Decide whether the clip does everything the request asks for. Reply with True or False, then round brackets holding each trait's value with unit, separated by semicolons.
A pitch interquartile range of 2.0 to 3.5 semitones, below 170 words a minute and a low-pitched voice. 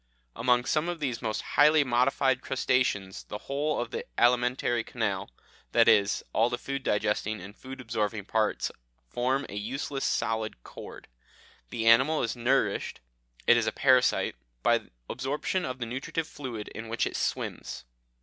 True (3.2 semitones; 155 wpm; 120 Hz)